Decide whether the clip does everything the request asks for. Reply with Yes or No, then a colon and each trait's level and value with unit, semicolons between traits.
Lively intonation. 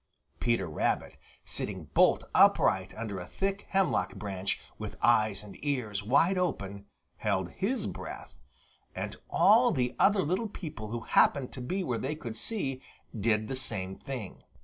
Yes: wide, 8.8 semitones